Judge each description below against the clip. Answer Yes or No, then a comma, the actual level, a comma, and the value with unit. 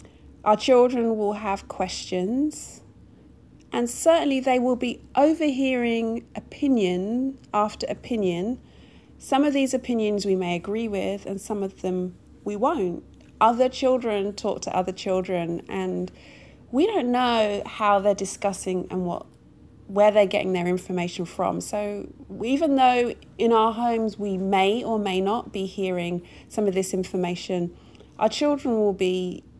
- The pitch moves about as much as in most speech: Yes, average, 4.5 semitones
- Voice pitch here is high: Yes, high, 210 Hz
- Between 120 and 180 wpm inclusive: Yes, average, 140 wpm